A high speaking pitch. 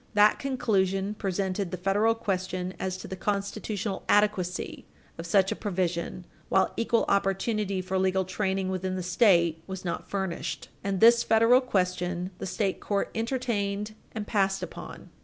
Yes: high, 195 Hz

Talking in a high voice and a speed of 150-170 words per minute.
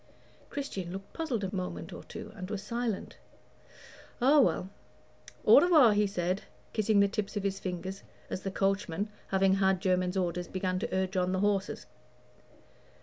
Yes: high, 195 Hz; average, 160 wpm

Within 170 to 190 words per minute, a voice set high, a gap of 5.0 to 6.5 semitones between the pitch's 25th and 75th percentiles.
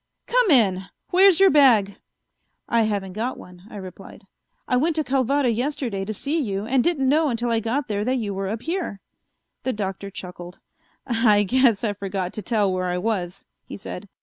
Yes: average, 185 wpm; high, 220 Hz; wide, 5.4 semitones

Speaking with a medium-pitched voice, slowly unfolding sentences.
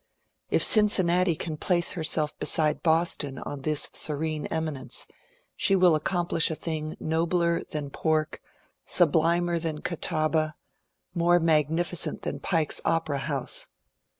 Yes: medium, 160 Hz; slow, 120 wpm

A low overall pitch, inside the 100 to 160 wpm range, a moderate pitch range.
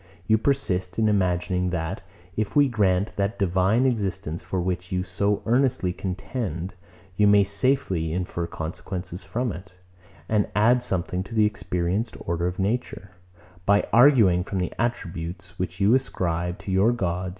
Yes: very low, 95 Hz; average, 150 wpm; average, 3.4 semitones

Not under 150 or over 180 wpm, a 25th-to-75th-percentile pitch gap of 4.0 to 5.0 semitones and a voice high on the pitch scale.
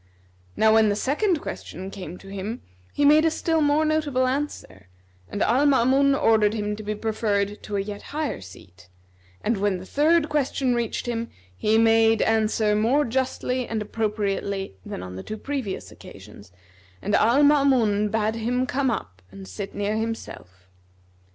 Yes: average, 165 wpm; average, 4.7 semitones; high, 220 Hz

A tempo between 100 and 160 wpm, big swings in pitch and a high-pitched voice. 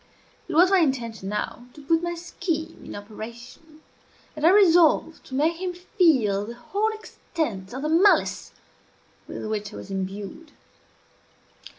Yes: average, 150 wpm; wide, 7.9 semitones; very high, 305 Hz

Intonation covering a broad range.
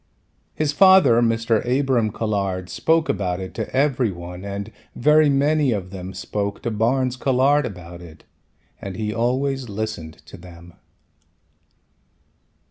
Yes: wide, 6.1 semitones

